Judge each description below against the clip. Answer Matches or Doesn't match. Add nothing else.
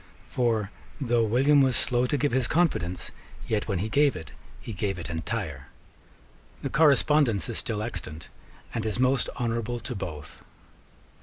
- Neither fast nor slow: Matches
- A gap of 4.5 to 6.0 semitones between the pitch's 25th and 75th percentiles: Matches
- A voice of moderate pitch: Doesn't match